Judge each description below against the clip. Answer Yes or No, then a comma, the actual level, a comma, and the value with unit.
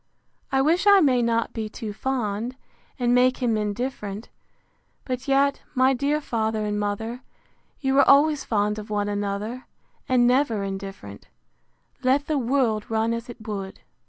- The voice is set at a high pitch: Yes, high, 235 Hz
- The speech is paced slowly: No, average, 155 wpm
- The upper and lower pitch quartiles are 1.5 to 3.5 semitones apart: No, average, 4.0 semitones